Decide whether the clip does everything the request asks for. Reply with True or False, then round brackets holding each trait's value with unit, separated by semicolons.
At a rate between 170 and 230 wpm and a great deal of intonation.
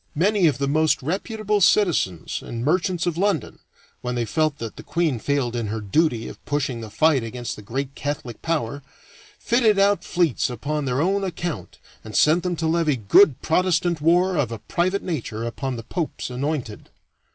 True (180 wpm; 6.2 semitones)